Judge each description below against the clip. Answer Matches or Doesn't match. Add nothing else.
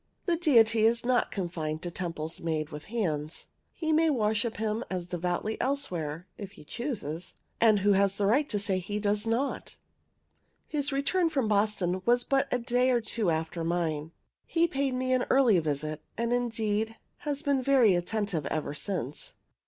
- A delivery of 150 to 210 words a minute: Matches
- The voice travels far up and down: Matches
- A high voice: Matches